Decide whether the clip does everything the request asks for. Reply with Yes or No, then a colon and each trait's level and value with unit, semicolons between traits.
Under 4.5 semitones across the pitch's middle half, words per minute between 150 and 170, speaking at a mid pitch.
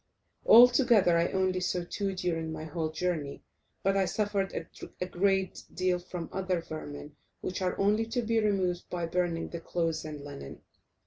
Yes: average, 2.9 semitones; average, 165 wpm; medium, 180 Hz